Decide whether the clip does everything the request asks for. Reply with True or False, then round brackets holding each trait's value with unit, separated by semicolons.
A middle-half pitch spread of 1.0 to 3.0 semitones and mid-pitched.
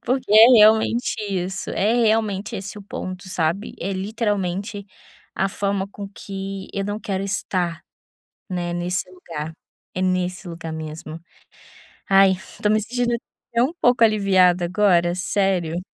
False (2.7 semitones; 195 Hz)